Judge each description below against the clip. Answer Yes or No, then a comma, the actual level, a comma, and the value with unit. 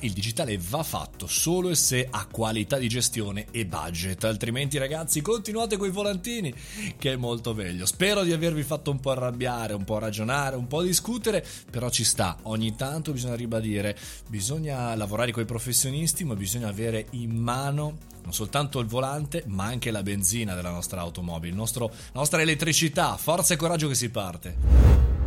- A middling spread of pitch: No, wide, 5.8 semitones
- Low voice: Yes, low, 120 Hz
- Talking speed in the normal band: No, fast, 175 wpm